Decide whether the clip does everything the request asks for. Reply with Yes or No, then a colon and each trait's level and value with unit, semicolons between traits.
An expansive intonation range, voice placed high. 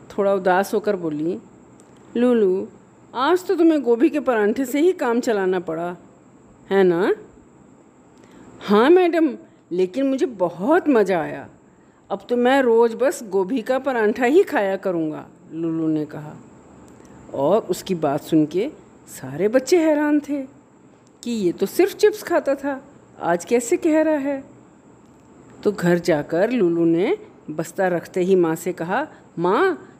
Yes: wide, 8.5 semitones; high, 235 Hz